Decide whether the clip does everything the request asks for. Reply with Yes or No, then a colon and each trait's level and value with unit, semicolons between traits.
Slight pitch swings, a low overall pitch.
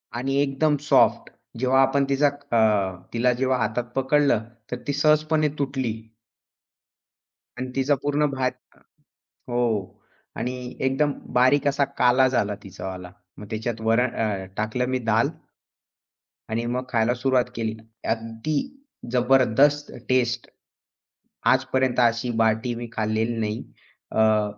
No: average, 3.1 semitones; low, 125 Hz